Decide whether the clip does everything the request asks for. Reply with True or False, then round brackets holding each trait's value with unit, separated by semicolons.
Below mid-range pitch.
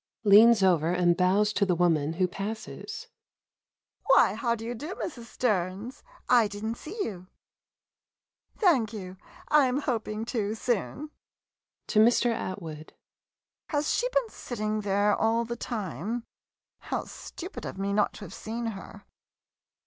False (215 Hz)